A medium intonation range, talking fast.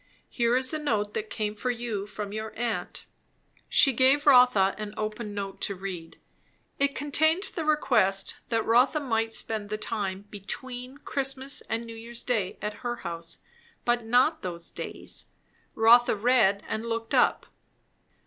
No: average, 3.5 semitones; average, 155 wpm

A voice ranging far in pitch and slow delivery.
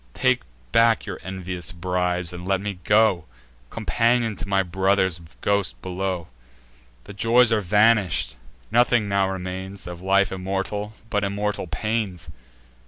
No: narrow, 2.4 semitones; slow, 130 wpm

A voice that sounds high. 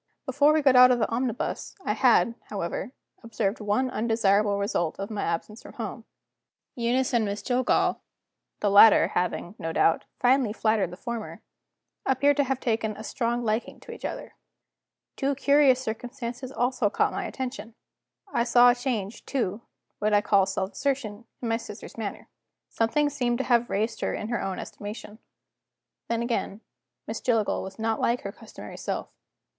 Yes: high, 230 Hz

